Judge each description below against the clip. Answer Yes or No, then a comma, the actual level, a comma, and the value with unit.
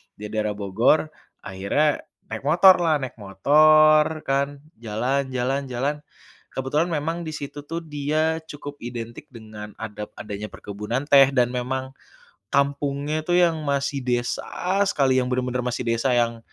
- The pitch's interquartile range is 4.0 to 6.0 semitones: Yes, average, 4.3 semitones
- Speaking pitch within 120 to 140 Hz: Yes, low, 135 Hz